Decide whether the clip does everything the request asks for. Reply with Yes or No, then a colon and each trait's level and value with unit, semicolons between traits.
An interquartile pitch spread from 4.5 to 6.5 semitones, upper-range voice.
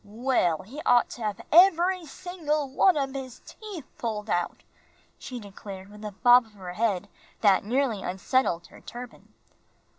Yes: wide, 5.6 semitones; high, 240 Hz